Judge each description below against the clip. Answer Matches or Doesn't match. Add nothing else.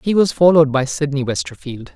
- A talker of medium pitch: Matches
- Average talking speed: Matches